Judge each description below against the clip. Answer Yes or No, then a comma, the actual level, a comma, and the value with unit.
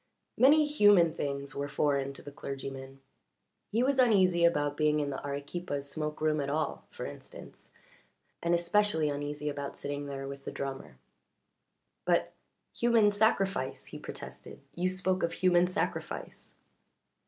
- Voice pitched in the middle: Yes, medium, 150 Hz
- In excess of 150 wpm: No, average, 140 wpm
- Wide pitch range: No, average, 4.7 semitones